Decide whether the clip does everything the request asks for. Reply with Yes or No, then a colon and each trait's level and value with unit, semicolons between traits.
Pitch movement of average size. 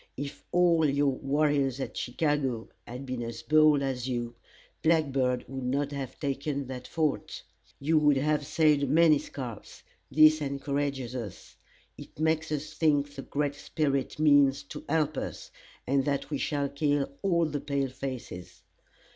No: narrow, 2.3 semitones